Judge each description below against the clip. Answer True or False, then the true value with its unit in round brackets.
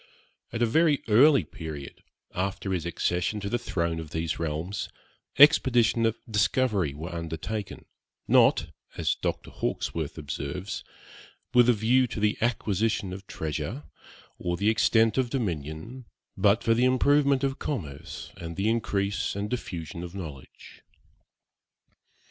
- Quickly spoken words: False (135 wpm)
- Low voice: True (100 Hz)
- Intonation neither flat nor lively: False (6.3 semitones)